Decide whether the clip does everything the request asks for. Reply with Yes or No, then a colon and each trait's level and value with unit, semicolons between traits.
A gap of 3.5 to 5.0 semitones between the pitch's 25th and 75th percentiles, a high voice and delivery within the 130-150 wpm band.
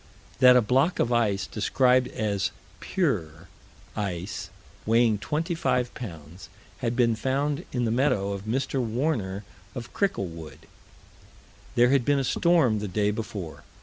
No: average, 4.7 semitones; low, 115 Hz; slow, 135 wpm